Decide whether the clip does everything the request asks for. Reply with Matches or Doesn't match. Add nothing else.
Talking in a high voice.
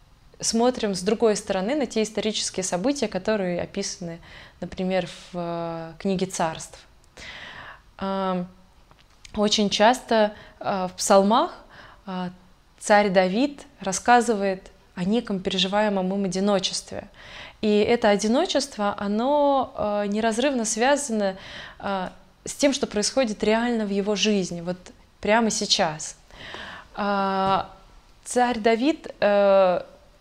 Matches